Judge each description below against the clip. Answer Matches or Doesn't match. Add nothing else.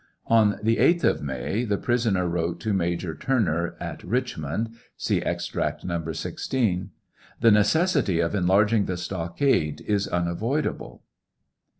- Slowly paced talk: Matches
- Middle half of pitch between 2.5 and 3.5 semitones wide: Doesn't match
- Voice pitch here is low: Matches